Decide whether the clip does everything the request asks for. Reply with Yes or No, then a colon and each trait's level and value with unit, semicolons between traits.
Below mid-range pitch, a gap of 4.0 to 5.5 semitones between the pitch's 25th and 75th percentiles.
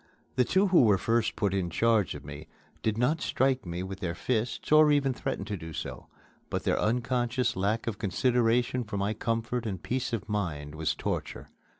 Yes: low, 115 Hz; average, 4.6 semitones